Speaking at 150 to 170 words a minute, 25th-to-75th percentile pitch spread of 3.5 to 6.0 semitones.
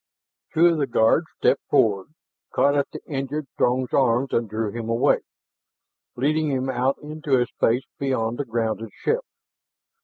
Yes: average, 155 wpm; average, 3.9 semitones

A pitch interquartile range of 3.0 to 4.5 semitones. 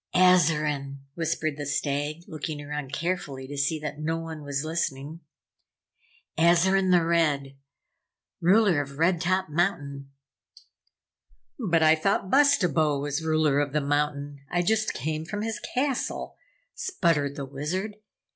Yes: average, 3.5 semitones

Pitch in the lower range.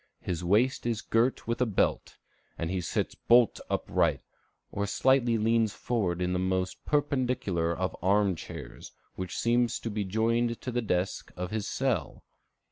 Yes: low, 110 Hz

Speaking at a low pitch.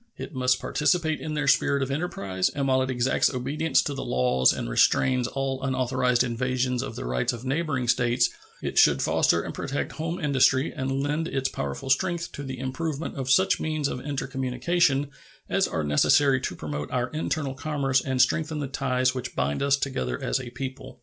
Yes: low, 130 Hz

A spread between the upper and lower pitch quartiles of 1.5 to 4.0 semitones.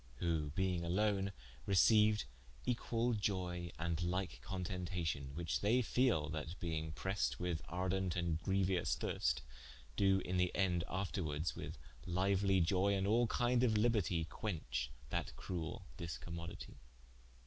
Yes: average, 2.9 semitones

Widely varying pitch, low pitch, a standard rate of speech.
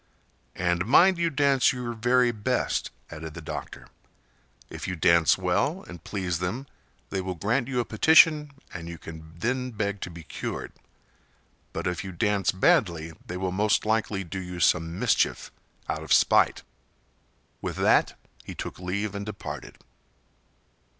Yes: wide, 5.7 semitones; very low, 95 Hz; average, 155 wpm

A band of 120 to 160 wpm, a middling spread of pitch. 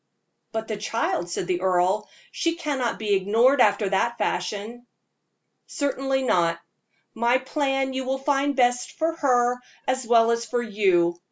Yes: average, 150 wpm; average, 4.7 semitones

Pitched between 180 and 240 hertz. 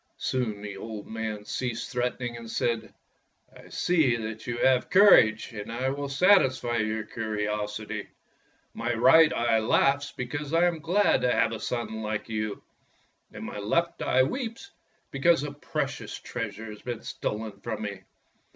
No: low, 115 Hz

